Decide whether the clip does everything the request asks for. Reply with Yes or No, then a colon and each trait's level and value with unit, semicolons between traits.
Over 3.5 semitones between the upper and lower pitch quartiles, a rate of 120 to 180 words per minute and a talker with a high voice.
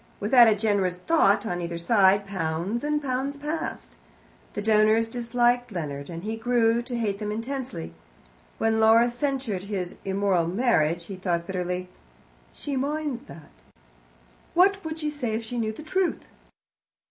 Yes: average, 5.0 semitones; average, 150 wpm; high, 220 Hz